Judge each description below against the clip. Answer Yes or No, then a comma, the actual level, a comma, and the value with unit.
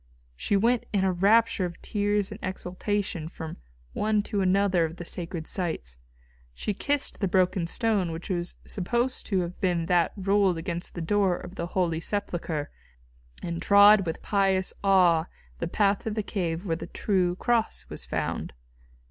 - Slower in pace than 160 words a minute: No, average, 165 wpm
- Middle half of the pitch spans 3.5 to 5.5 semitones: No, average, 3.0 semitones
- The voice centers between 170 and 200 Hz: Yes, medium, 185 Hz